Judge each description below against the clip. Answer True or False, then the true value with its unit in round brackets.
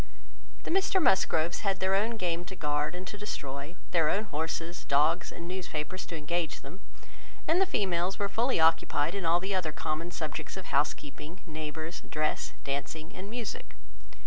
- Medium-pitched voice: True (170 Hz)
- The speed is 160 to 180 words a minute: True (170 wpm)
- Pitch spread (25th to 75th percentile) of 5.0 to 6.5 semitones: False (3.8 semitones)